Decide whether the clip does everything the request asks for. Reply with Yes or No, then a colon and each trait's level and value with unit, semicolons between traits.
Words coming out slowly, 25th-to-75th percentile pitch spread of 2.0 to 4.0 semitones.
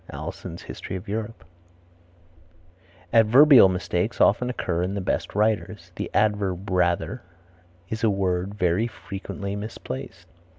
Yes: slow, 120 wpm; average, 3.2 semitones